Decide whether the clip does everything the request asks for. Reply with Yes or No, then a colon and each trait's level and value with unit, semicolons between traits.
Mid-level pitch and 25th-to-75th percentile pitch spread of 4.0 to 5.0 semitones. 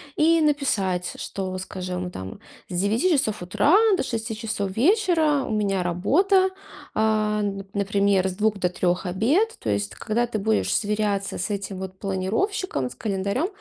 No: high, 205 Hz; average, 4.7 semitones